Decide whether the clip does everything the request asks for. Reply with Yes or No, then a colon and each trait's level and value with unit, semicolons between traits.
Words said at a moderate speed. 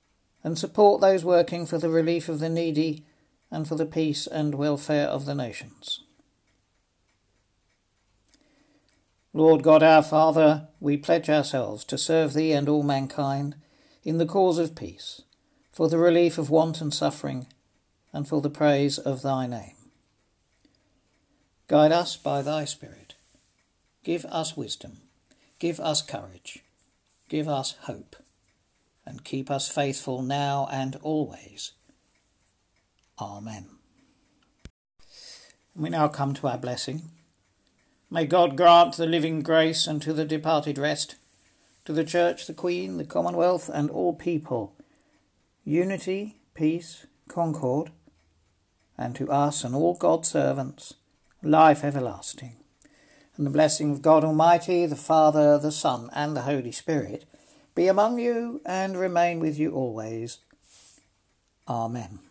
No: slow, 130 wpm